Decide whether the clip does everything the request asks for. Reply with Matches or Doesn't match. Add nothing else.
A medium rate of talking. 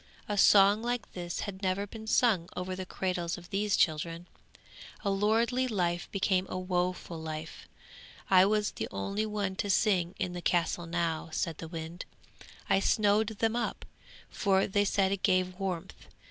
Matches